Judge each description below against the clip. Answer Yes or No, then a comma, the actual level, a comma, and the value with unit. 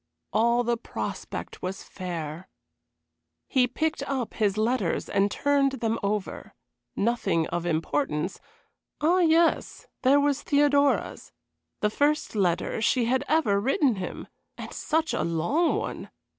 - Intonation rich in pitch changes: Yes, wide, 6.7 semitones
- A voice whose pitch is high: Yes, high, 235 Hz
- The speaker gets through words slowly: Yes, slow, 130 wpm